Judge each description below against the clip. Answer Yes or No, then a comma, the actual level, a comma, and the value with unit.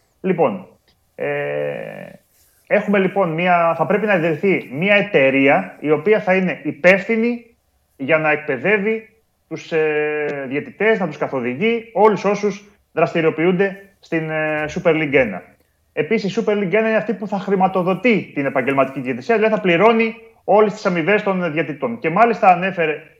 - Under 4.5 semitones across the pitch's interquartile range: No, average, 5.1 semitones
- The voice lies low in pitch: No, medium, 185 Hz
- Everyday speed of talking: Yes, average, 145 wpm